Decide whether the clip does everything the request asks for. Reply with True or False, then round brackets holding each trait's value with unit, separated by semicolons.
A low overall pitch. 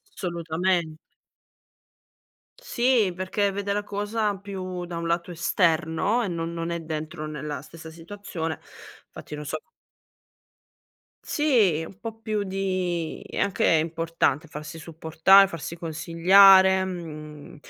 False (170 Hz)